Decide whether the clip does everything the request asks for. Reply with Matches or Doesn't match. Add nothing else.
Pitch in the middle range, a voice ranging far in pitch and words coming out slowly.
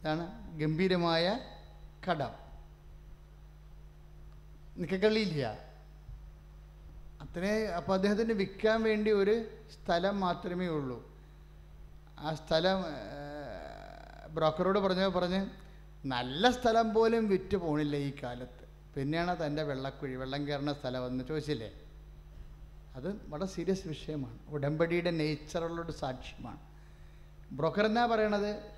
Matches